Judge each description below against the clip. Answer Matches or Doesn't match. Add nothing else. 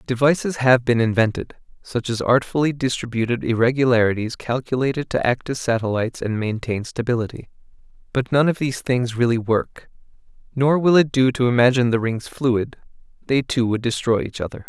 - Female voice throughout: Doesn't match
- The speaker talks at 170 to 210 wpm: Doesn't match